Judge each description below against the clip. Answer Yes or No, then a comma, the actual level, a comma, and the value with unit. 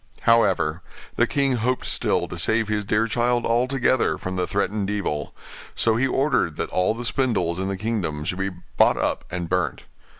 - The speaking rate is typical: Yes, average, 180 wpm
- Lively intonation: No, average, 4.6 semitones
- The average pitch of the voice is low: Yes, low, 105 Hz